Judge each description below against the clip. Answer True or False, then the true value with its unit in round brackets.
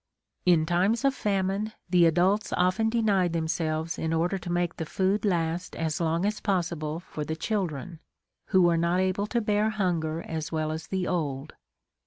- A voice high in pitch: False (175 Hz)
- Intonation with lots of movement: False (3.4 semitones)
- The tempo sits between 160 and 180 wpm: True (175 wpm)